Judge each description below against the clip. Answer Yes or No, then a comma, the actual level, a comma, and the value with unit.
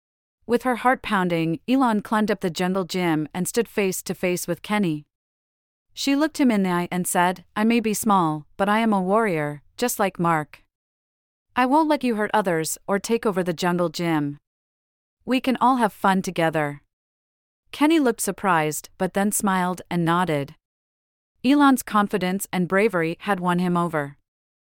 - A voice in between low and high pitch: Yes, medium, 180 Hz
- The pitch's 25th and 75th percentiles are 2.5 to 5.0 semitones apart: No, wide, 5.6 semitones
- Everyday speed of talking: Yes, average, 175 wpm